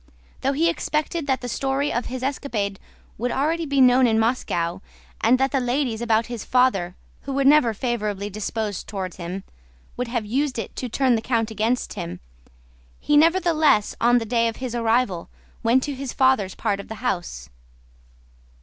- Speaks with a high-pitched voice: Yes, high, 240 Hz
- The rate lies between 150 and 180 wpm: Yes, average, 170 wpm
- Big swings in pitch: No, average, 4.1 semitones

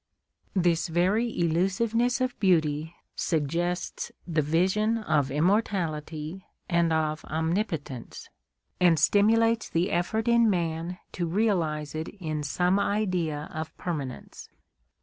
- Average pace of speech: No, slow, 110 wpm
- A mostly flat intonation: No, average, 4.3 semitones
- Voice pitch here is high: No, medium, 175 Hz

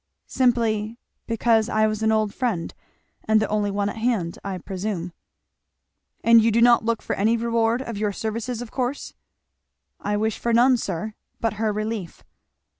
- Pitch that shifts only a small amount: Yes, narrow, 1.9 semitones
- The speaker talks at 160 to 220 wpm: Yes, average, 170 wpm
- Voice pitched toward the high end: Yes, high, 220 Hz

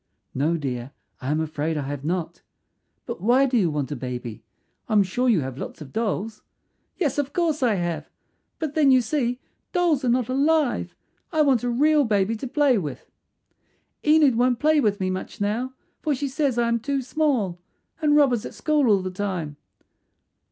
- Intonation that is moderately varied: No, wide, 8.2 semitones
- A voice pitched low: No, high, 235 Hz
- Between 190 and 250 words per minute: Yes, average, 195 wpm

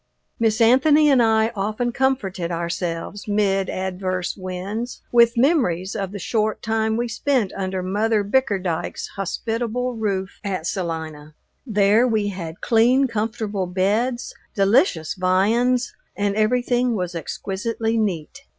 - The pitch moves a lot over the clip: No, average, 4.0 semitones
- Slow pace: Yes, slow, 125 wpm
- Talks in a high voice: Yes, high, 210 Hz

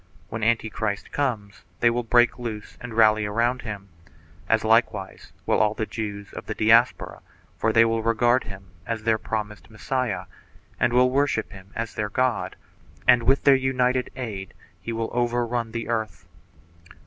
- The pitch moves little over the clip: Yes, narrow, 2.2 semitones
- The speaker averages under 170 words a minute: Yes, average, 160 wpm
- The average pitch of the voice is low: Yes, low, 115 Hz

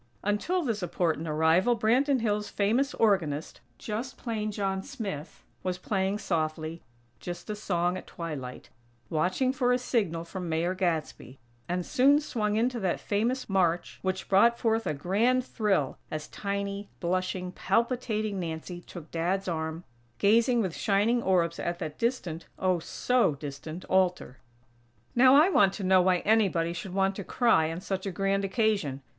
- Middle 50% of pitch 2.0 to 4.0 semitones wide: No, average, 4.5 semitones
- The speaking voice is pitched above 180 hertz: Yes, high, 190 Hz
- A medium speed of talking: Yes, average, 155 wpm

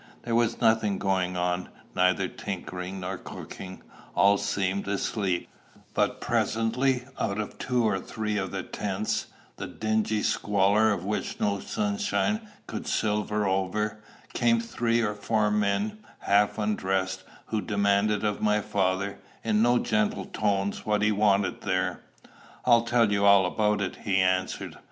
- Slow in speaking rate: No, average, 145 wpm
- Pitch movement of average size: No, narrow, 2.2 semitones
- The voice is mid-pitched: No, low, 105 Hz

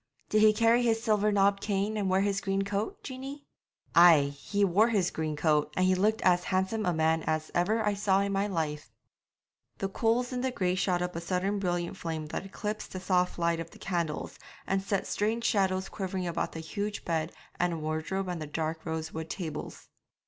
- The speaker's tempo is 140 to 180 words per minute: No, average, 200 wpm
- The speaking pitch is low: No, high, 190 Hz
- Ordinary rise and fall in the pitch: Yes, average, 3.7 semitones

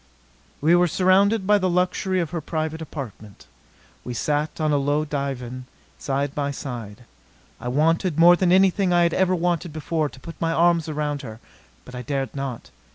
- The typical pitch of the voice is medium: Yes, medium, 155 Hz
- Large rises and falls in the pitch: No, average, 4.1 semitones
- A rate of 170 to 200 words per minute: Yes, average, 180 wpm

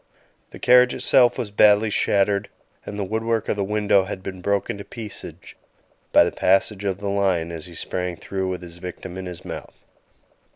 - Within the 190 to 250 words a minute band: Yes, average, 195 wpm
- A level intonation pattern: Yes, narrow, 2.1 semitones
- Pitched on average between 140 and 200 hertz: No, low, 100 Hz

